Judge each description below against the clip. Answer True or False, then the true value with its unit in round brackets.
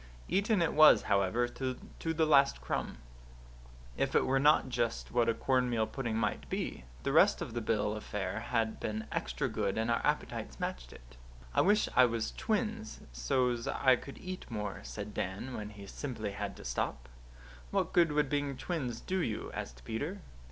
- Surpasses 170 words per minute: True (180 wpm)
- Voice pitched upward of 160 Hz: False (120 Hz)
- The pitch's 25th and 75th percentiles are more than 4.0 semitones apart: True (5.5 semitones)